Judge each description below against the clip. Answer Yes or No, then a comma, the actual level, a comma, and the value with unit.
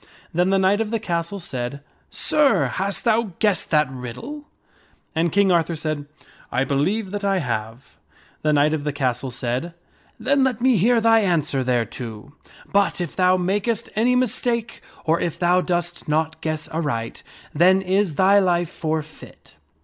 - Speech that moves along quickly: No, average, 170 wpm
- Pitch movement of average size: No, wide, 5.7 semitones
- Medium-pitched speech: Yes, medium, 175 Hz